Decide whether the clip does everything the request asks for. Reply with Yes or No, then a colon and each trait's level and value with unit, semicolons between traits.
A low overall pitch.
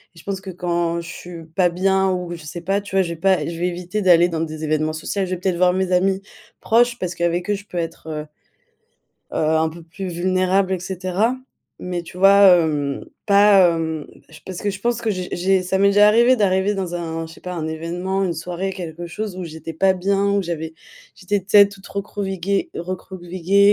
No: medium, 180 Hz